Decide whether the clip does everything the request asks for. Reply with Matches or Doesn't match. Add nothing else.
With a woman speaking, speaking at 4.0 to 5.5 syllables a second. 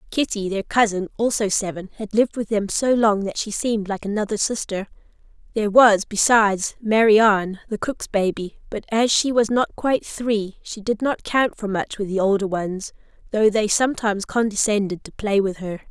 Matches